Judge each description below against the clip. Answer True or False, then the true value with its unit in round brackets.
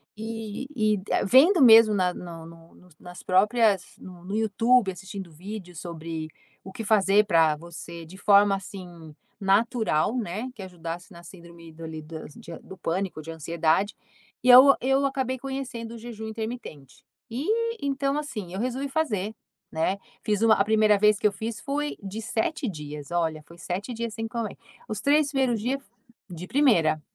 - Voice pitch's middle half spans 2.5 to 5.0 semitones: False (5.4 semitones)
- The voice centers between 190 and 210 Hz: True (205 Hz)